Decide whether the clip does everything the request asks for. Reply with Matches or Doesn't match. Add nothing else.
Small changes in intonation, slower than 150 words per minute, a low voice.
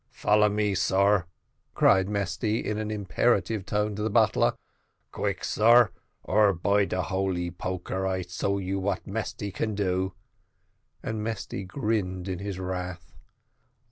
Matches